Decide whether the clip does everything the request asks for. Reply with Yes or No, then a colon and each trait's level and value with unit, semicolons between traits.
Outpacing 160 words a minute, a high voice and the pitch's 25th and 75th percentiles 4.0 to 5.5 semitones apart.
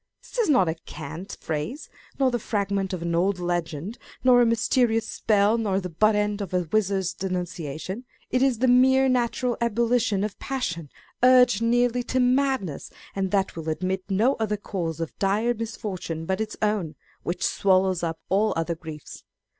Yes: average, 170 wpm; high, 200 Hz; average, 5.1 semitones